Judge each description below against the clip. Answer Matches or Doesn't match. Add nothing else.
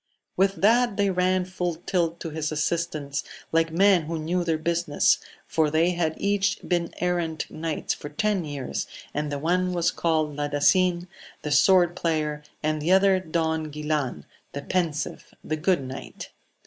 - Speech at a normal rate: Matches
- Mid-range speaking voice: Matches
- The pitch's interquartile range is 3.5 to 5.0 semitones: Doesn't match